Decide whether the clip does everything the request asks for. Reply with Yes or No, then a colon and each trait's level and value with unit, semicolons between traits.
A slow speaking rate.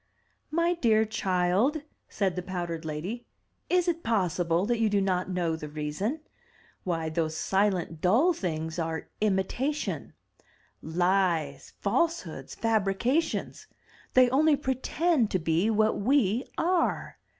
Yes: slow, 125 wpm